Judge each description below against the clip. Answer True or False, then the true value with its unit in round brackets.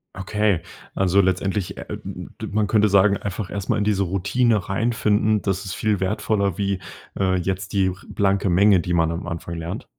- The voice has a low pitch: True (100 Hz)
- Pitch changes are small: True (2.0 semitones)